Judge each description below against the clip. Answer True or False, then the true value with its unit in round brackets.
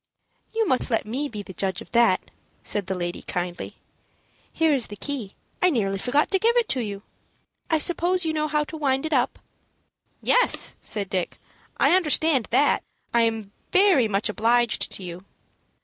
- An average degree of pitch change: False (7.5 semitones)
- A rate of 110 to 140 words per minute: False (180 wpm)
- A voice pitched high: True (245 Hz)